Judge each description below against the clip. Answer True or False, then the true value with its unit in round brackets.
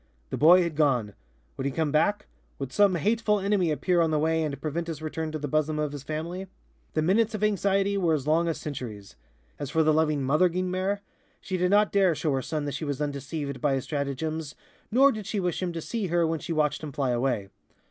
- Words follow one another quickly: True (230 wpm)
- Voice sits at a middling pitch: True (160 Hz)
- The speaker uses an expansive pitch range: False (4.0 semitones)